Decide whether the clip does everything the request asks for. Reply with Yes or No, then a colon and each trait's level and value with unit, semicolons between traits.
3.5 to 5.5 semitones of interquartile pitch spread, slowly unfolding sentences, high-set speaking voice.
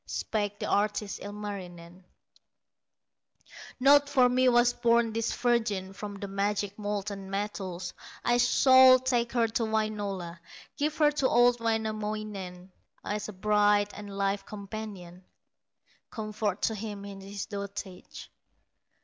No: narrow, 2.6 semitones; slow, 125 wpm; high, 210 Hz